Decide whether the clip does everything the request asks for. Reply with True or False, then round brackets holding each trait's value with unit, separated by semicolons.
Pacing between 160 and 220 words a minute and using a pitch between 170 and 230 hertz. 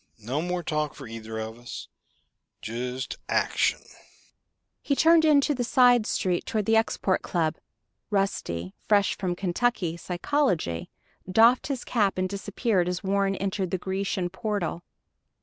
False (135 wpm; 190 Hz)